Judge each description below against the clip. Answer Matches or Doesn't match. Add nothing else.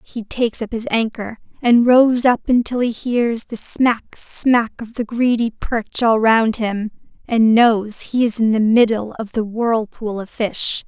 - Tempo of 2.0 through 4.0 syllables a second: Matches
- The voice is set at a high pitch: Matches